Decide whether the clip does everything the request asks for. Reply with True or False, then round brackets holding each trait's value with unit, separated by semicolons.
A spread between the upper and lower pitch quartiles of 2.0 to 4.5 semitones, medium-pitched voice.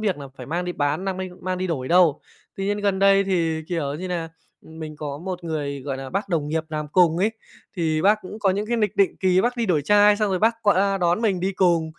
True (3.8 semitones; 180 Hz)